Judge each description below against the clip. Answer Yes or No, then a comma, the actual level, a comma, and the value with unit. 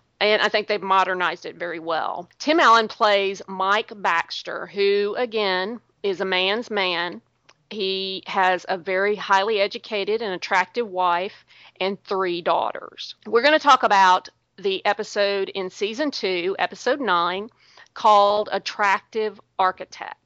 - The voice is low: No, high, 200 Hz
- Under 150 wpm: Yes, slow, 135 wpm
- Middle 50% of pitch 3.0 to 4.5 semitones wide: No, narrow, 2.4 semitones